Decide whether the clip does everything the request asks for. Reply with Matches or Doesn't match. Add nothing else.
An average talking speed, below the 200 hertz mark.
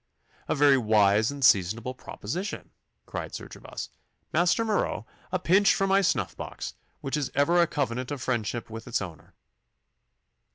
Matches